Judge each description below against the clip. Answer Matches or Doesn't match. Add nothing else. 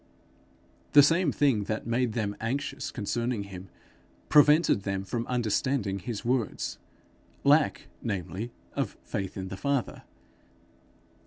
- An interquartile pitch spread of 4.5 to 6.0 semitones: Matches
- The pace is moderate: Doesn't match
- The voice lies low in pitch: Matches